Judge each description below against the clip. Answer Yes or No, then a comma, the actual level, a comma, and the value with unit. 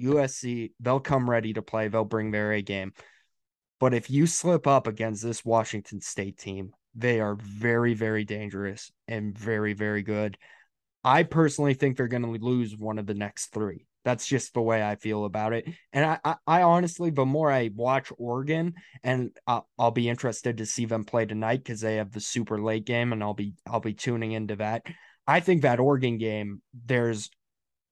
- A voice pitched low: Yes, low, 115 Hz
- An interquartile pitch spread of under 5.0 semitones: Yes, average, 3.4 semitones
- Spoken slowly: No, average, 195 wpm